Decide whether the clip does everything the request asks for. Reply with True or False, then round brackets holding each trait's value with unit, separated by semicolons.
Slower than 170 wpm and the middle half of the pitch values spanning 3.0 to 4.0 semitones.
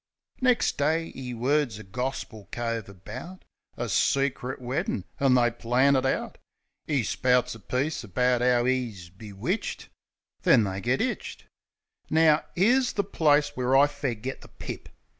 True (150 wpm; 3.7 semitones)